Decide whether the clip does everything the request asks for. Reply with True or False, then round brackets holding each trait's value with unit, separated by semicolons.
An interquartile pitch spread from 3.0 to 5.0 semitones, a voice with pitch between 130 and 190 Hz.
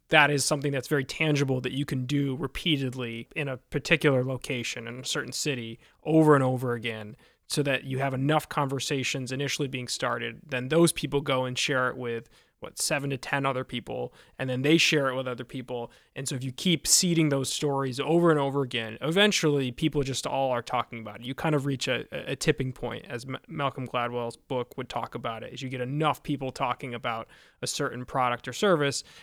False (2.6 semitones; 135 Hz)